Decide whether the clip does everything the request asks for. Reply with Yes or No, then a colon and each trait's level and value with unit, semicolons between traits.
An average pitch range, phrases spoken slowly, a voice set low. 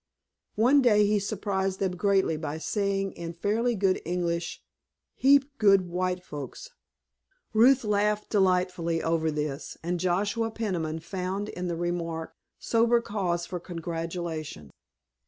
No: average, 3.6 semitones; slow, 125 wpm; medium, 185 Hz